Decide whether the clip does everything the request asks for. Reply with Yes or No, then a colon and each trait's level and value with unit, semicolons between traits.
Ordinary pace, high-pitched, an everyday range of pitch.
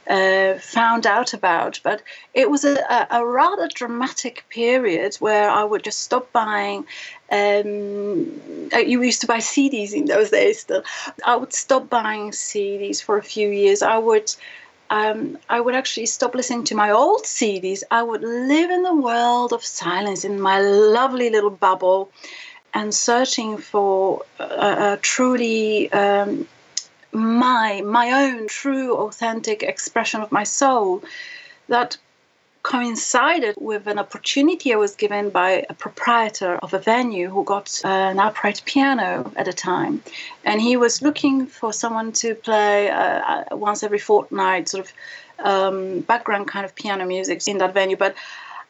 Yes: average, 155 wpm; high, 225 Hz; average, 4.4 semitones